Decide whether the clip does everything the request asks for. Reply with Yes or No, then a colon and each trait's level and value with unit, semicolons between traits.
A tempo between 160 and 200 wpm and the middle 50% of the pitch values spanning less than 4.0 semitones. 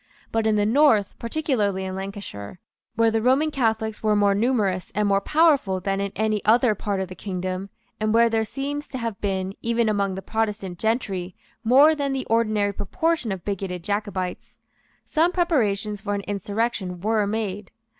Yes: average, 175 wpm; average, 2.9 semitones